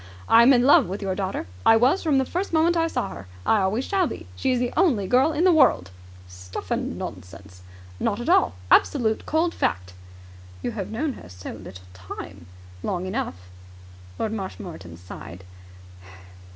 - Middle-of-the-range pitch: No, high, 215 Hz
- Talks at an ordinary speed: Yes, average, 180 wpm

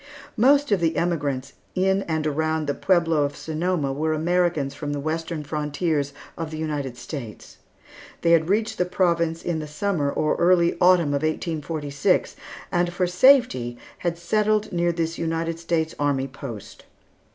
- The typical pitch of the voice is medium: Yes, medium, 160 Hz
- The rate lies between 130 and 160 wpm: Yes, average, 155 wpm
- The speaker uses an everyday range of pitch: Yes, average, 3.0 semitones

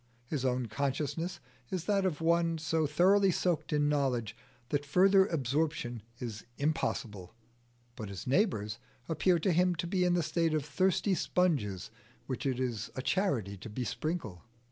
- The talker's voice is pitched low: No, medium, 150 Hz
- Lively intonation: Yes, wide, 6.0 semitones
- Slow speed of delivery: No, average, 155 wpm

